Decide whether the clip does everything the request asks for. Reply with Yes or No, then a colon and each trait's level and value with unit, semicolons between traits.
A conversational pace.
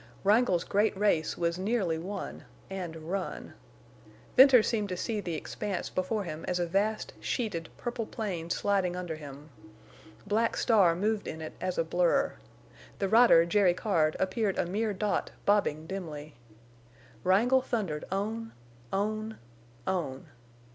No: slow, 130 wpm